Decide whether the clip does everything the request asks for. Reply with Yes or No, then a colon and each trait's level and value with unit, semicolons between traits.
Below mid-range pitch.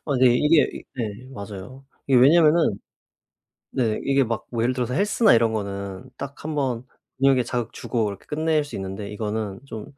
Yes: low, 125 Hz